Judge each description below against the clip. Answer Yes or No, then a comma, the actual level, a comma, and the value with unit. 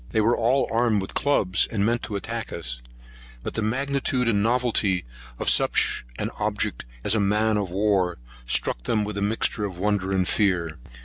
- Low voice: Yes, low, 105 Hz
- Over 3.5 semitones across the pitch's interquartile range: No, average, 3.2 semitones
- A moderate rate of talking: Yes, average, 185 wpm